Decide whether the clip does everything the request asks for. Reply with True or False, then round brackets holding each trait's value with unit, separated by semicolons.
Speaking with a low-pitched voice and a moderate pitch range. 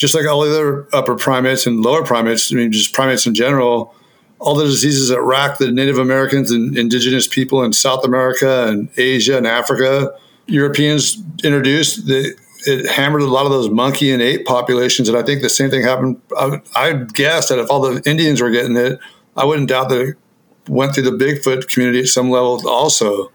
False (130 Hz; 1.9 semitones)